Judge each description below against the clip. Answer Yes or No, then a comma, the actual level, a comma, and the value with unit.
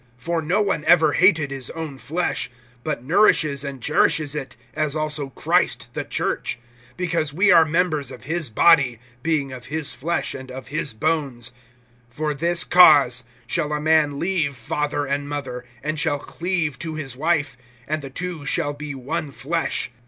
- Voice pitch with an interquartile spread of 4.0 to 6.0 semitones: No, average, 2.9 semitones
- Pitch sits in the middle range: Yes, medium, 150 Hz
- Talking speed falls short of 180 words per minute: Yes, average, 165 wpm